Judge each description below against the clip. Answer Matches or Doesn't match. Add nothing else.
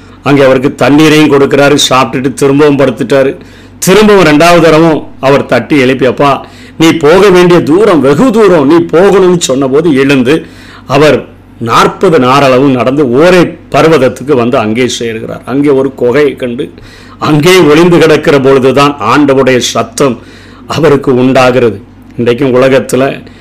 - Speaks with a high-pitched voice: Doesn't match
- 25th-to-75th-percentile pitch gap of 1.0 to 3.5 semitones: Matches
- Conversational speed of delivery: Matches